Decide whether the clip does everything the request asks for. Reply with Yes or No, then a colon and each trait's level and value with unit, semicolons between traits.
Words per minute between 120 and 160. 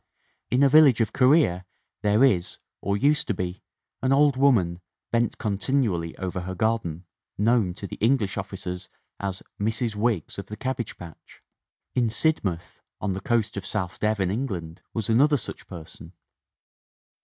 Yes: average, 155 wpm